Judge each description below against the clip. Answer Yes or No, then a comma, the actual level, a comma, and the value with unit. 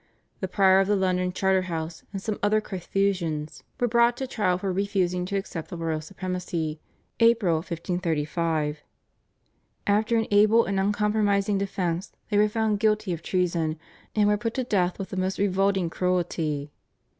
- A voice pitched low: No, high, 190 Hz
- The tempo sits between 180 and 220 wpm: No, average, 155 wpm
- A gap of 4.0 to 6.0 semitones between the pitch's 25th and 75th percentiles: No, average, 3.2 semitones